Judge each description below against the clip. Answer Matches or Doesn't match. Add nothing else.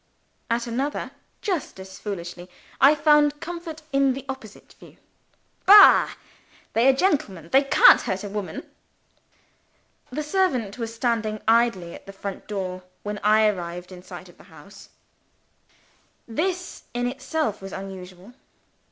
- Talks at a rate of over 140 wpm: Doesn't match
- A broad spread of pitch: Matches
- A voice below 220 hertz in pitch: Doesn't match